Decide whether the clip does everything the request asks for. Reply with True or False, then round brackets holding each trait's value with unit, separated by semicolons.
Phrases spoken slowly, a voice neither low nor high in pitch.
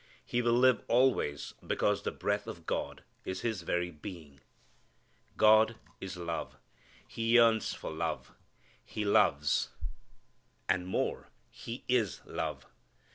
False (125 wpm; 105 Hz)